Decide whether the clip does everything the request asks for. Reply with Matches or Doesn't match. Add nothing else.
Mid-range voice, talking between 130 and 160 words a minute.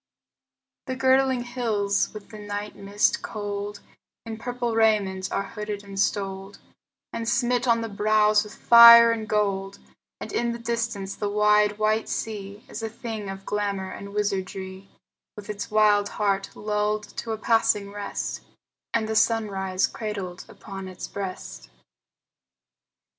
Doesn't match